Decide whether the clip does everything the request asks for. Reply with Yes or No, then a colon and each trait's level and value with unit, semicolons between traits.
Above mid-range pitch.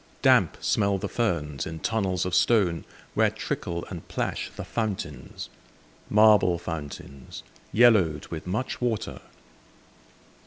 No: very low, 90 Hz